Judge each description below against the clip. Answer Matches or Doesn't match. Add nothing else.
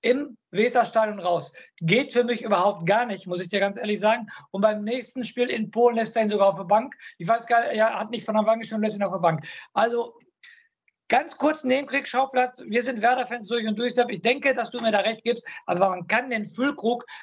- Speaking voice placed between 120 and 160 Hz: Doesn't match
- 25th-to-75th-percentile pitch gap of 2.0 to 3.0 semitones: Matches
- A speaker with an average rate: Doesn't match